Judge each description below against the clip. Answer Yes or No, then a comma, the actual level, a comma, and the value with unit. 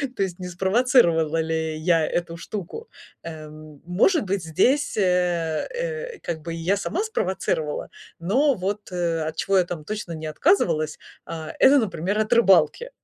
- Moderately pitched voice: Yes, medium, 180 Hz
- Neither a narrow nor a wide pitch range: No, wide, 6.1 semitones